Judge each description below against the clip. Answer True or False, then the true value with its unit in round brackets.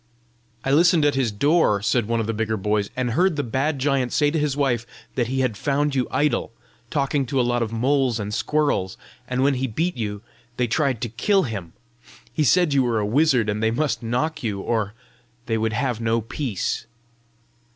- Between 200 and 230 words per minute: True (205 wpm)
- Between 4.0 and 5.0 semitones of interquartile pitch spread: True (4.3 semitones)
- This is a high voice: False (125 Hz)